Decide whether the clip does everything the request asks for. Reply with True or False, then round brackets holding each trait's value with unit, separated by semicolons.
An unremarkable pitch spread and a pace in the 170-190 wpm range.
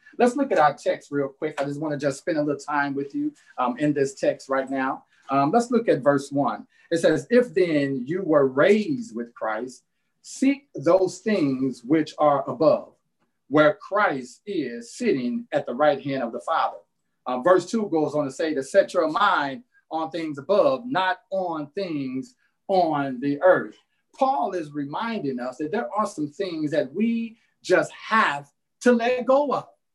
False (8.3 semitones; 185 wpm)